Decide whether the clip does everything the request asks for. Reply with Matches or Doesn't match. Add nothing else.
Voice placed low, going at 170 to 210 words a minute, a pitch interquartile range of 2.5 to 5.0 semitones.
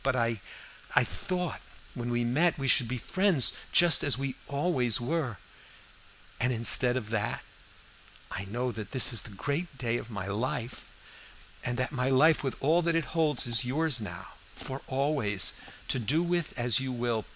Matches